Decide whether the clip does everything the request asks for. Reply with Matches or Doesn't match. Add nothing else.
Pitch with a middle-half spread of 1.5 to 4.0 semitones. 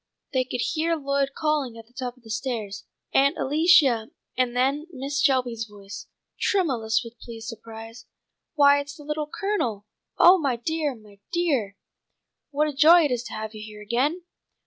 Doesn't match